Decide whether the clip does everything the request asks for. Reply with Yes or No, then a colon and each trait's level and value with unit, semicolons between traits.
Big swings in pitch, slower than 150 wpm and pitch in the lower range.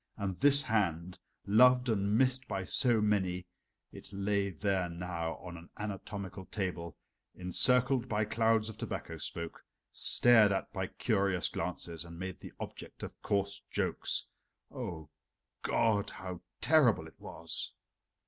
No: average, 3.8 semitones; slow, 135 wpm; low, 100 Hz